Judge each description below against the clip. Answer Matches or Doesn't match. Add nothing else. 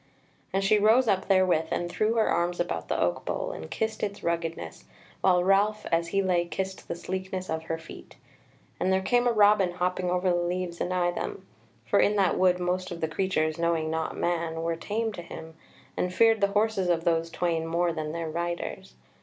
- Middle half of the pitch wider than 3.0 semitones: Doesn't match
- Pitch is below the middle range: Doesn't match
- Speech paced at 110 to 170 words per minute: Doesn't match